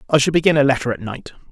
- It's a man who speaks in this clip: Yes, male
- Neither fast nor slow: No, fast, 275 wpm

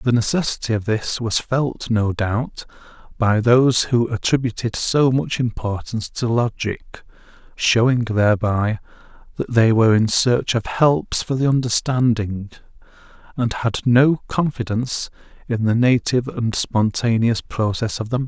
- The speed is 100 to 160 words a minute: Yes, average, 140 wpm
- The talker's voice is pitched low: Yes, low, 115 Hz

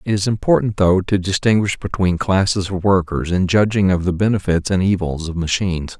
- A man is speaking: Yes, male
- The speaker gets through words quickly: No, average, 190 wpm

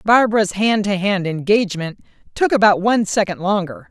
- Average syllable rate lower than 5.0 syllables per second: No, 5.5 syllables/s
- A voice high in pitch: Yes, high, 200 Hz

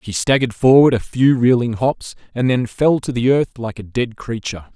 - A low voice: Yes, low, 120 Hz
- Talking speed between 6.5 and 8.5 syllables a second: No, 5.2 syllables/s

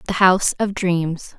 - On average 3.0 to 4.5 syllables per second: Yes, 4.3 syllables/s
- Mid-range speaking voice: Yes, medium, 180 Hz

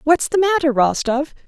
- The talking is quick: No, average, 165 wpm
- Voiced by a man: No, female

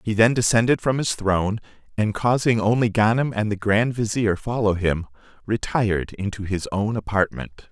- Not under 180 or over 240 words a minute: No, average, 165 wpm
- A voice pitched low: Yes, low, 110 Hz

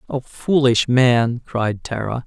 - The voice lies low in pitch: Yes, low, 120 Hz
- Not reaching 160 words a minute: Yes, slow, 135 wpm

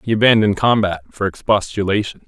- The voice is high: No, low, 105 Hz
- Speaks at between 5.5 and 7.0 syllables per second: Yes, 6.1 syllables/s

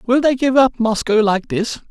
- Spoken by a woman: No, male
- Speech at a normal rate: No, fast, 220 wpm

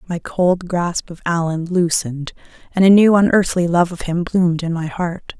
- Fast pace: No, average, 190 wpm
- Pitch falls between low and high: Yes, medium, 175 Hz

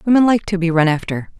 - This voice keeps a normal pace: No, fast, 260 wpm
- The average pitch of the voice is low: No, medium, 185 Hz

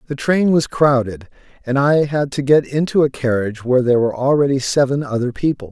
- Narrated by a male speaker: Yes, male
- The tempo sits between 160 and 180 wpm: No, average, 200 wpm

